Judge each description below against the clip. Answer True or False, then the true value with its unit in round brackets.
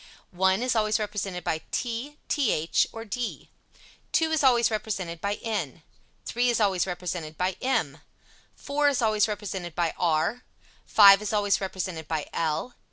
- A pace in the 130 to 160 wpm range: True (155 wpm)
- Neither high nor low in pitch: False (205 Hz)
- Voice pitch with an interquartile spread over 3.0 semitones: True (4.7 semitones)